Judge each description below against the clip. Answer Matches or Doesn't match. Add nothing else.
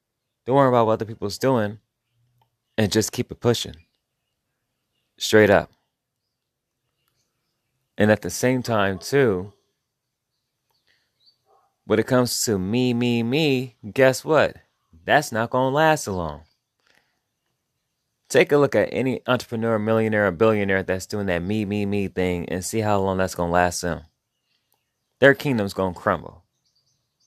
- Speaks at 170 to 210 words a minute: Doesn't match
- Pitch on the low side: Matches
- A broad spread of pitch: Doesn't match